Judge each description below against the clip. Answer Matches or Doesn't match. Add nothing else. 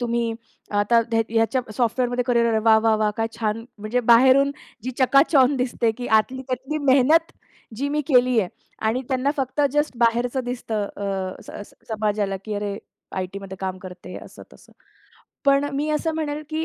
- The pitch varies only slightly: Doesn't match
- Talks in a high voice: Matches